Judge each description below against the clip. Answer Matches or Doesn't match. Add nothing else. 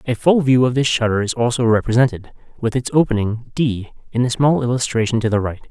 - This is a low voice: Matches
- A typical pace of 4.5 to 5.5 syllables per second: Doesn't match